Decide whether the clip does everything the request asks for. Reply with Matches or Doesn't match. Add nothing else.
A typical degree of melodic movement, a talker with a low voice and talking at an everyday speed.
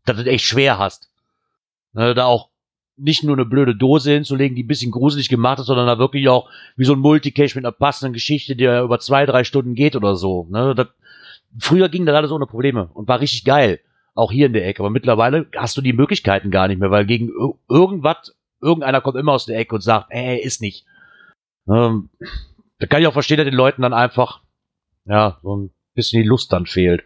Doesn't match